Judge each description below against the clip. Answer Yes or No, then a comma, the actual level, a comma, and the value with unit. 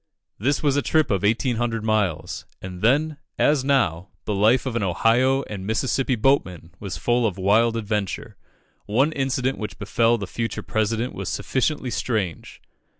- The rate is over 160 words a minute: No, average, 155 wpm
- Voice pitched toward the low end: Yes, low, 115 Hz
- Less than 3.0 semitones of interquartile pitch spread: No, average, 4.4 semitones